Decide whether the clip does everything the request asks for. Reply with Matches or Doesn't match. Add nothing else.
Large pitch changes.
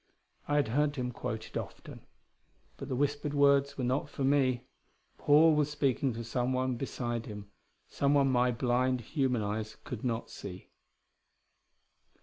Doesn't match